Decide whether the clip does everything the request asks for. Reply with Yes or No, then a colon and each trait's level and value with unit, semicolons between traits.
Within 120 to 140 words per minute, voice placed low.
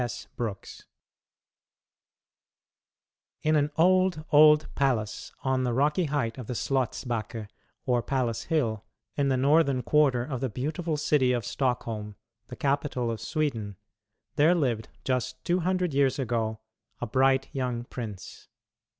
Yes: slow, 135 wpm; low, 130 Hz